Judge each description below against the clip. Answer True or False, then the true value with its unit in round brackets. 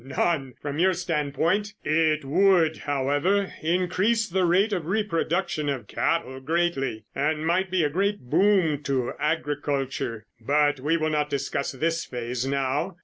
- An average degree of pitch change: True (4.3 semitones)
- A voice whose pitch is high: False (155 Hz)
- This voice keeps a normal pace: True (145 wpm)